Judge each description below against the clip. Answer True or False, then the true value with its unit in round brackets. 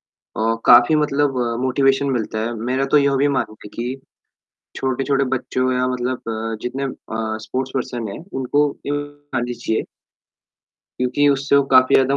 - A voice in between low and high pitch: False (130 Hz)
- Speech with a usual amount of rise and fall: False (2.3 semitones)